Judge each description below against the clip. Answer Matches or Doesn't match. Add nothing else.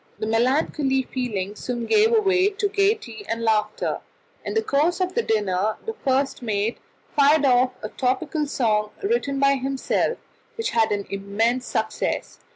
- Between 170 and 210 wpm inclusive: Doesn't match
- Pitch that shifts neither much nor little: Doesn't match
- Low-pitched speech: Doesn't match